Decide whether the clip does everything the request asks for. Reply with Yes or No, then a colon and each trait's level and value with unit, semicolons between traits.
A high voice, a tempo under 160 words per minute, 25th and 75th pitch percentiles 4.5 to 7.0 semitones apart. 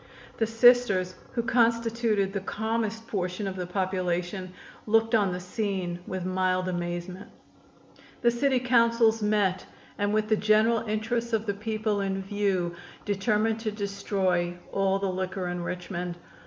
No: high, 200 Hz; average, 140 wpm; average, 3.4 semitones